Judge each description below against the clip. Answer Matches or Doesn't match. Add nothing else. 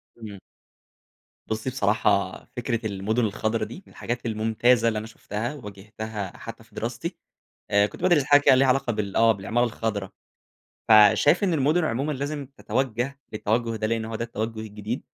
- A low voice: Matches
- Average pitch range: Matches